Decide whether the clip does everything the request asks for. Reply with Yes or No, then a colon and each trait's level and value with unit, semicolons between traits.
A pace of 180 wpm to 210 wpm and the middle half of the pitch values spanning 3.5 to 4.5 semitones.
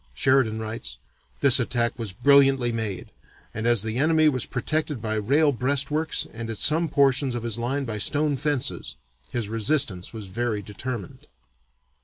No: average, 155 wpm; average, 4.2 semitones